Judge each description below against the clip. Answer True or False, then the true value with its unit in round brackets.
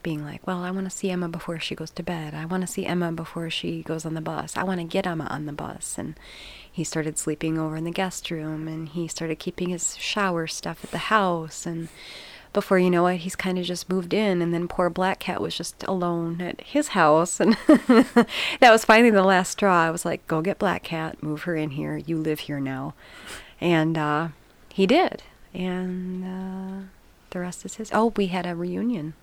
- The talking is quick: True (225 wpm)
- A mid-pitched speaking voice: True (175 Hz)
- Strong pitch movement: False (2.8 semitones)